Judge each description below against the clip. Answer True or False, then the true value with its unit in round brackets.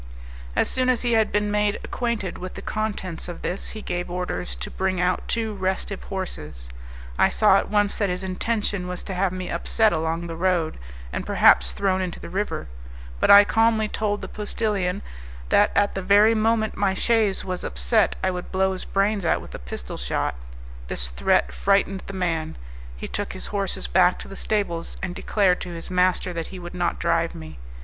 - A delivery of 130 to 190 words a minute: False (200 wpm)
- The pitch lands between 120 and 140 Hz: False (190 Hz)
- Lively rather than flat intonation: False (2.9 semitones)